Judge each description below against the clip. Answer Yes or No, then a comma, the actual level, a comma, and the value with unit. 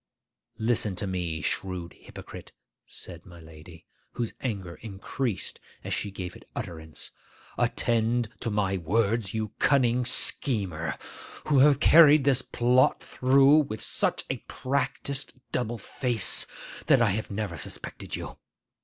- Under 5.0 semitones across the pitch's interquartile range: No, wide, 5.5 semitones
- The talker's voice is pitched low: Yes, low, 110 Hz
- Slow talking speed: Yes, slow, 130 wpm